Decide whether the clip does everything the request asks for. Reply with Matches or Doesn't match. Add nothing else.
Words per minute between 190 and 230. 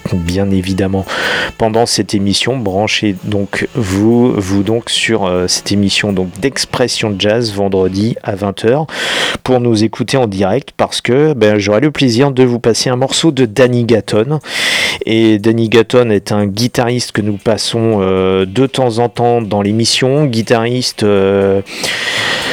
Doesn't match